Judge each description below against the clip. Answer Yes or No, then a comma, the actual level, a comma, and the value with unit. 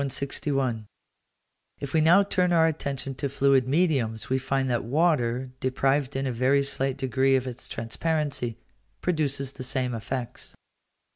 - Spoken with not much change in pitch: Yes, narrow, 2.3 semitones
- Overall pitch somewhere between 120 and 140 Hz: Yes, low, 135 Hz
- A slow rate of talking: No, average, 145 wpm